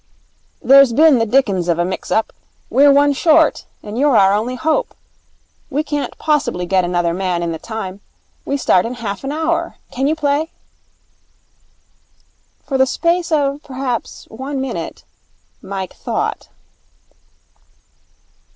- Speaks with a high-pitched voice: Yes, very high, 265 Hz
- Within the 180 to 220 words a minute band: No, average, 140 wpm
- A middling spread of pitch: No, wide, 6.6 semitones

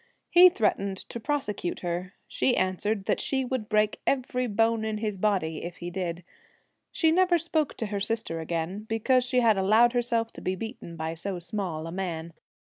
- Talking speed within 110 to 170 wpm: No, average, 185 wpm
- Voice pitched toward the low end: No, high, 210 Hz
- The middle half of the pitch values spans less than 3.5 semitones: No, average, 5.1 semitones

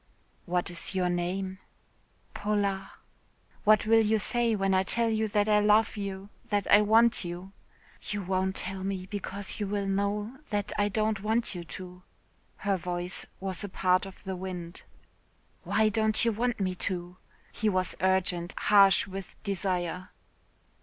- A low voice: No, high, 195 Hz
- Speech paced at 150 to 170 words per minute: Yes, average, 160 wpm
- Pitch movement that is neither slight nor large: No, narrow, 2.2 semitones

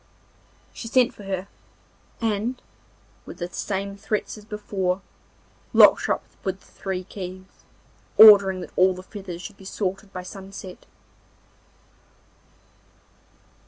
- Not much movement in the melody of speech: Yes, narrow, 1.9 semitones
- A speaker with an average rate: No, slow, 125 wpm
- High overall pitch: Yes, high, 195 Hz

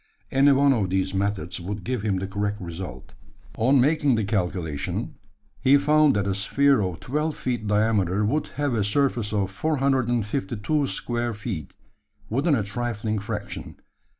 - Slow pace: No, average, 150 wpm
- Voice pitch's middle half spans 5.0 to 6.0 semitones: Yes, average, 5.3 semitones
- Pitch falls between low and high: No, low, 110 Hz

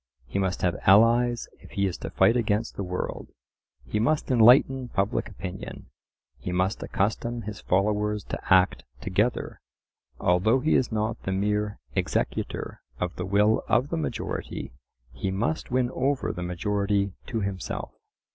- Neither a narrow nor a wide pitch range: Yes, average, 3.7 semitones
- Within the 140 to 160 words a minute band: Yes, average, 150 wpm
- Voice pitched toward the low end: Yes, low, 105 Hz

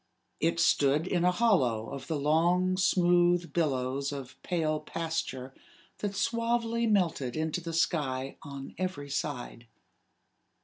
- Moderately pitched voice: Yes, medium, 165 Hz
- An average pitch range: Yes, average, 4.6 semitones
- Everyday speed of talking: No, slow, 125 wpm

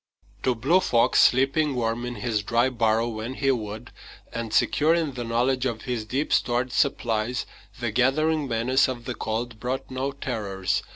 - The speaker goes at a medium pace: Yes, average, 170 wpm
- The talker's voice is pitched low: Yes, low, 120 Hz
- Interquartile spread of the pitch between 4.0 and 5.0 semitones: No, narrow, 2.6 semitones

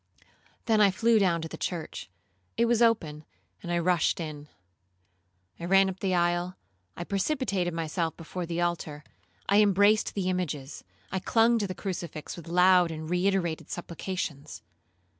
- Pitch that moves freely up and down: No, average, 2.8 semitones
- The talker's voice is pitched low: No, medium, 180 Hz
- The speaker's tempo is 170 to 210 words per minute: No, average, 155 wpm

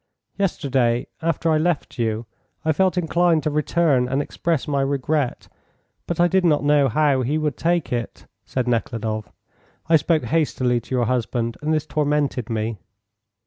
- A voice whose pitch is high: No, medium, 145 Hz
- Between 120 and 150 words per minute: No, average, 160 wpm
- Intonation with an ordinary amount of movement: Yes, average, 4.4 semitones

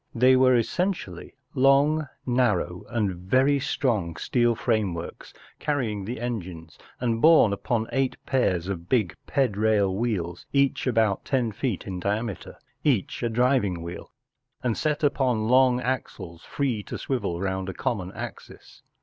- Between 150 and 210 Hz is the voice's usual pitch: No, low, 115 Hz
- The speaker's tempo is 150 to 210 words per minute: No, average, 140 wpm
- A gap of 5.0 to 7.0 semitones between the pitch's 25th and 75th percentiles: Yes, average, 5.3 semitones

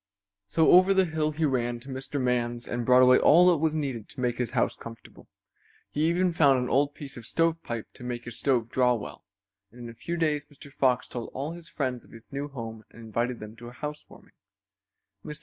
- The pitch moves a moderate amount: Yes, average, 4.1 semitones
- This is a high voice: No, low, 130 Hz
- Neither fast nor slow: No, fast, 220 wpm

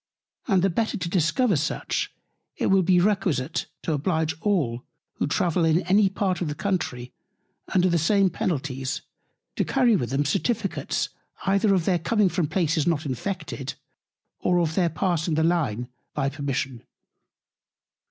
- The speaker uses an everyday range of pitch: Yes, average, 4.7 semitones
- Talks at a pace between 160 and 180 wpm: No, average, 150 wpm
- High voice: No, medium, 170 Hz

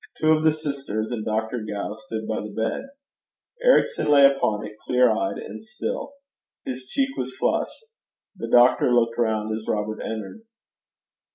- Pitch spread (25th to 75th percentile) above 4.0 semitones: Yes, average, 4.9 semitones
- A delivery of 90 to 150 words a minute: No, average, 160 wpm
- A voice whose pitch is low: Yes, low, 115 Hz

